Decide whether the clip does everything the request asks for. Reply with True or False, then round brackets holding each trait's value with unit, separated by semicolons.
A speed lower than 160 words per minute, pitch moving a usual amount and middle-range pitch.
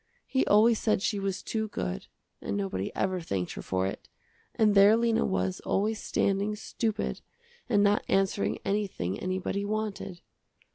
False (150 wpm; 3.5 semitones; 200 Hz)